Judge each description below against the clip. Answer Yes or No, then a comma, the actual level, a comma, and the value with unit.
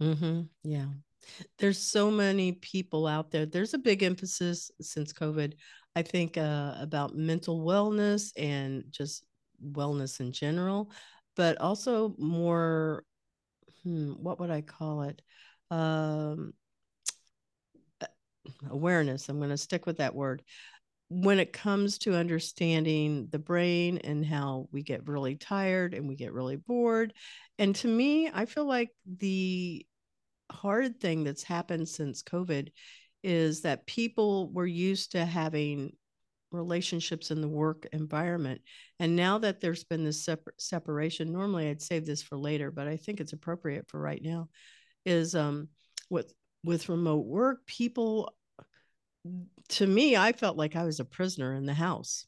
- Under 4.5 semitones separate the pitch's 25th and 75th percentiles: Yes, average, 3.9 semitones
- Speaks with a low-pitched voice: No, medium, 165 Hz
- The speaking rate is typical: Yes, average, 145 wpm